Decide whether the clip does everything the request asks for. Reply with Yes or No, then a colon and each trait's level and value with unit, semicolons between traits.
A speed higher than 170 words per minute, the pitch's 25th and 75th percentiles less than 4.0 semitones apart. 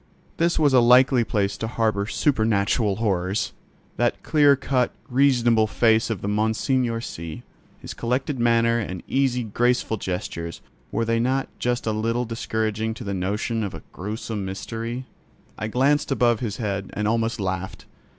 No: average, 150 wpm; average, 3.0 semitones